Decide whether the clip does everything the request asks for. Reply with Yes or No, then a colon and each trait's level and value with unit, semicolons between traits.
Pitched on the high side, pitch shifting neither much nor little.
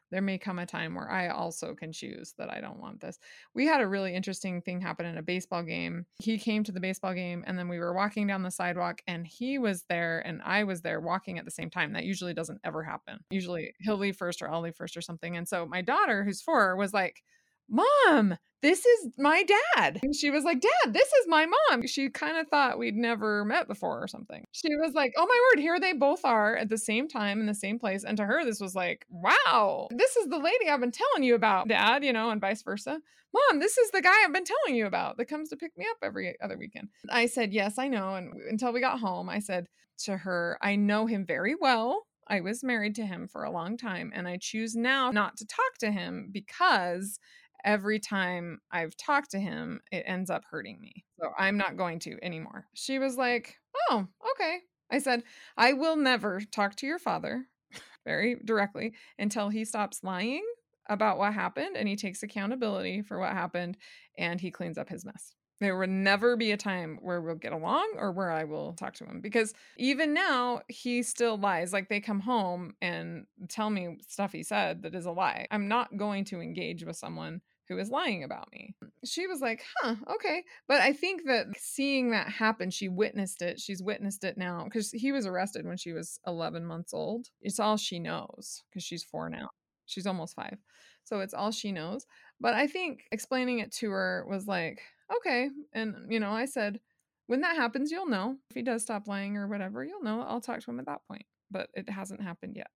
Yes: high, 215 Hz; average, 5.0 semitones